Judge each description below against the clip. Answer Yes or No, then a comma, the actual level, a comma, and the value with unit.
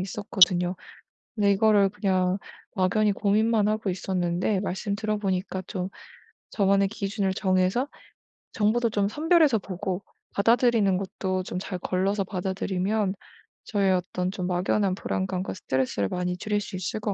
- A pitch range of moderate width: No, narrow, 2.3 semitones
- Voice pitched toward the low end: No, high, 195 Hz